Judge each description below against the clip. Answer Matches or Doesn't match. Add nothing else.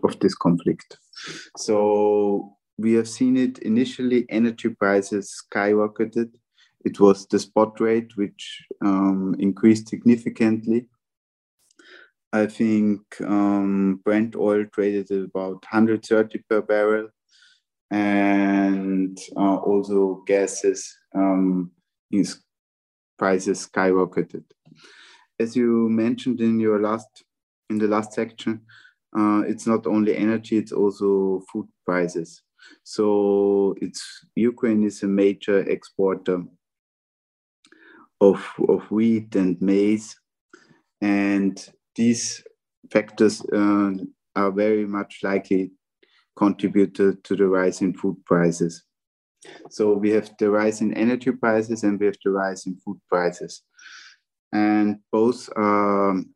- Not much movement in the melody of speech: Matches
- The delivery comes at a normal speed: Doesn't match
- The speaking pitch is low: Matches